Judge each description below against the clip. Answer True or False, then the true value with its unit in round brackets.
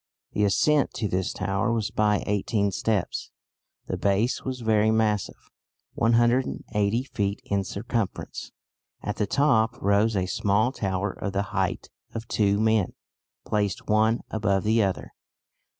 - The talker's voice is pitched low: True (105 Hz)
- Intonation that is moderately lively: False (2.2 semitones)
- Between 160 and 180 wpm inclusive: False (135 wpm)